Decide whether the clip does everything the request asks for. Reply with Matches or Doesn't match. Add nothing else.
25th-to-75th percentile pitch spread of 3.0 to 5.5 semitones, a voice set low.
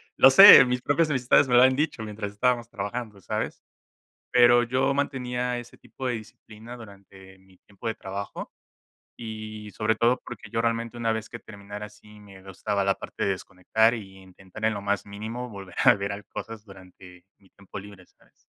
Matches